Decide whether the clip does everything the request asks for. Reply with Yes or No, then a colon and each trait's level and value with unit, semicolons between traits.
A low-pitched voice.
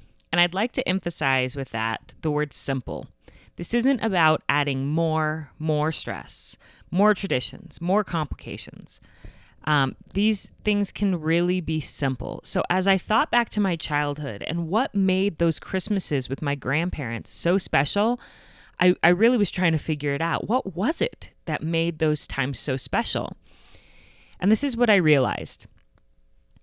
No: medium, 165 Hz